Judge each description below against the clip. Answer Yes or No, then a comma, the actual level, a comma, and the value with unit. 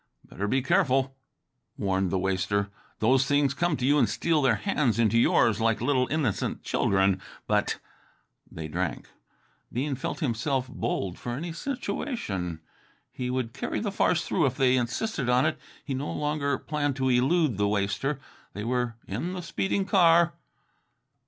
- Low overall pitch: Yes, low, 130 Hz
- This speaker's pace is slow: No, average, 160 wpm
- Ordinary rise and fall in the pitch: No, wide, 5.8 semitones